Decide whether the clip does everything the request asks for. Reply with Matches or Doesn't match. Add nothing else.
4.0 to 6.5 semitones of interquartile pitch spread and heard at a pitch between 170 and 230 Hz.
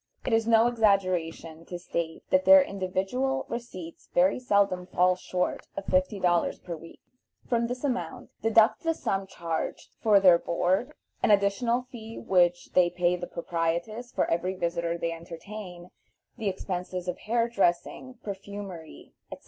Matches